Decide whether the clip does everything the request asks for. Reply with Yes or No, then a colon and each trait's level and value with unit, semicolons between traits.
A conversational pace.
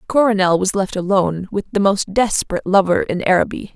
Yes: average, 175 wpm